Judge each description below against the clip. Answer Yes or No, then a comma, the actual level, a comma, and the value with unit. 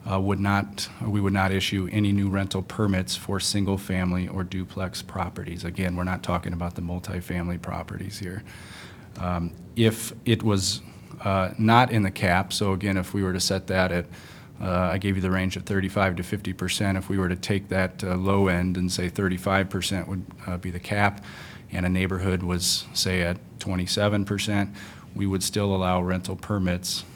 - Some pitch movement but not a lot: No, narrow, 1.7 semitones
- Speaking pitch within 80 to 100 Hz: Yes, very low, 95 Hz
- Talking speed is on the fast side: No, average, 190 wpm